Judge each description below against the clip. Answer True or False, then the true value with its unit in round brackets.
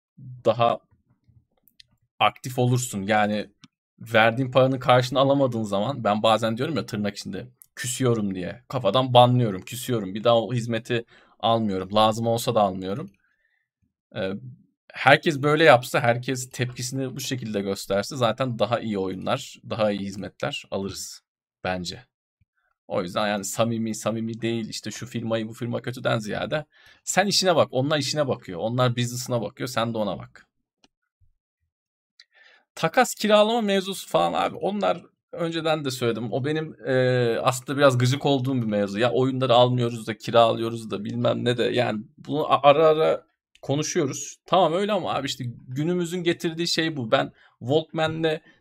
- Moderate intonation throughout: True (3.9 semitones)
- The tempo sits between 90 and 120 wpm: False (140 wpm)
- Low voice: True (120 Hz)